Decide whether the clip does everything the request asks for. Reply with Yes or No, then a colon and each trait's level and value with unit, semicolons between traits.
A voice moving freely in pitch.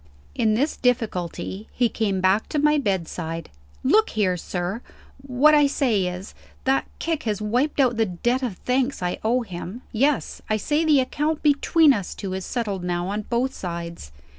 Yes: wide, 6.4 semitones